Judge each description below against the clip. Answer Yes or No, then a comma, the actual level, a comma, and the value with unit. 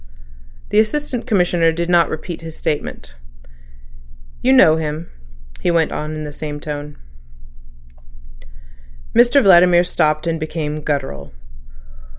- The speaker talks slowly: Yes, slow, 120 wpm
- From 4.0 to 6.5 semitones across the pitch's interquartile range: No, average, 2.8 semitones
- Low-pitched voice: No, medium, 160 Hz